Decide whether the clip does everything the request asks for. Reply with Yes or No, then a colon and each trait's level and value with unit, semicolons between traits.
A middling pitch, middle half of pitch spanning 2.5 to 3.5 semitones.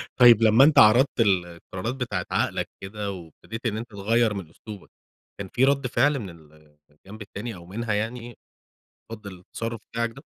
No: low, 110 Hz; average, 3.2 semitones